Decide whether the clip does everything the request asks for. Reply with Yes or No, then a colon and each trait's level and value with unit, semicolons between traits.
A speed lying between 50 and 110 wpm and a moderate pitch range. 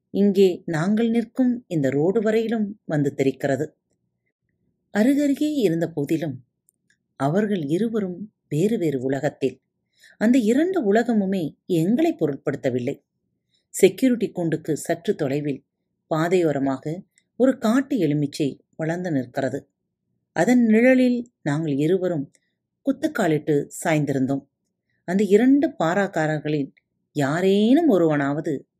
No: average, 90 wpm; wide, 7.5 semitones